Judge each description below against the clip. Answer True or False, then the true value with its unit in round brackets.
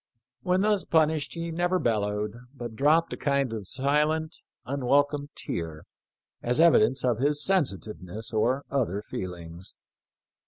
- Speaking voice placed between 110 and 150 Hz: True (135 Hz)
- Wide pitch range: True (6.6 semitones)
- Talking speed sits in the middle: False (125 wpm)